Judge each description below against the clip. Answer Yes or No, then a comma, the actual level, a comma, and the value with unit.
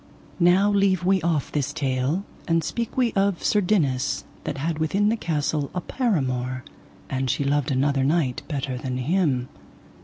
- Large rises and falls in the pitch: Yes, wide, 6.1 semitones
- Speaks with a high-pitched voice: No, medium, 155 Hz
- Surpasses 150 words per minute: Yes, average, 160 wpm